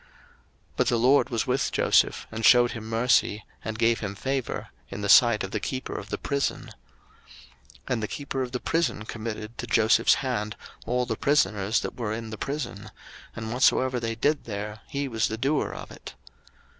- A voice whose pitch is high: No, low, 115 Hz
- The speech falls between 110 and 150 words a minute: No, average, 195 wpm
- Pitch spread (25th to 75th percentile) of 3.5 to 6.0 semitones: No, average, 3.0 semitones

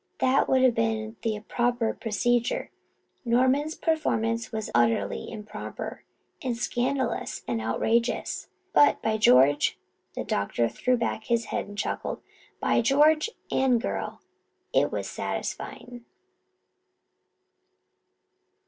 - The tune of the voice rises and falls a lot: No, average, 2.8 semitones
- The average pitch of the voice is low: No, high, 230 Hz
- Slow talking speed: Yes, slow, 110 wpm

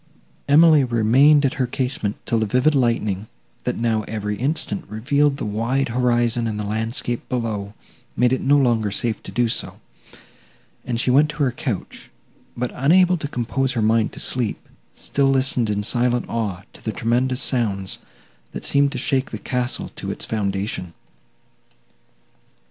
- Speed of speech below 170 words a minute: Yes, average, 160 wpm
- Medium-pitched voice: No, low, 120 Hz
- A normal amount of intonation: Yes, average, 3.5 semitones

